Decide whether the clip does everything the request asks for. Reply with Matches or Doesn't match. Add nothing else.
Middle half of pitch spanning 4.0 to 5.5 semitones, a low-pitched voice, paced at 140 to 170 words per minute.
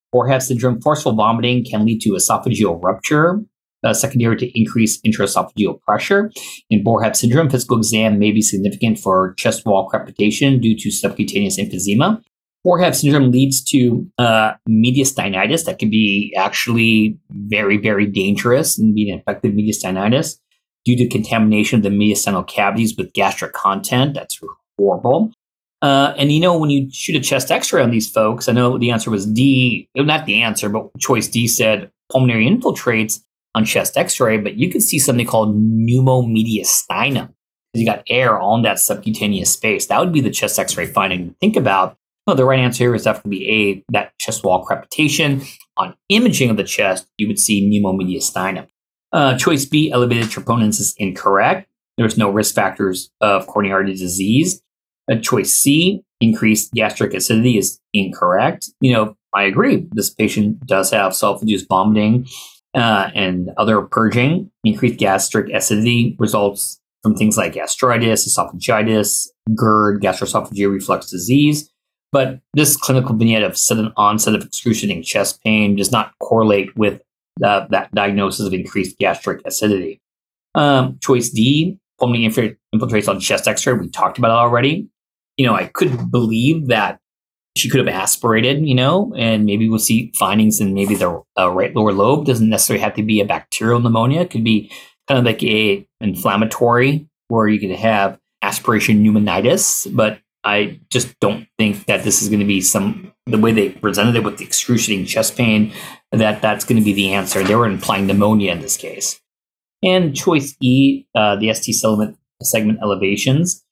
Doesn't match